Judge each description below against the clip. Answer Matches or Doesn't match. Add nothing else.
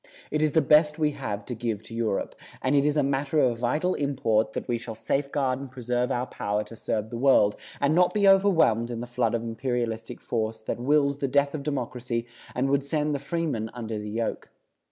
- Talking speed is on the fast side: Matches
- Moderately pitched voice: Doesn't match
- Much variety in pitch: Doesn't match